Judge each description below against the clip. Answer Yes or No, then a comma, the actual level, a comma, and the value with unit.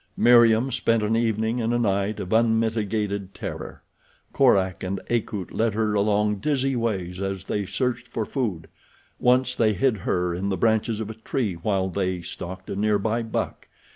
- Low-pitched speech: Yes, low, 110 Hz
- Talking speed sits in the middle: Yes, average, 170 wpm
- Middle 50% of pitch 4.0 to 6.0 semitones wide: No, average, 3.0 semitones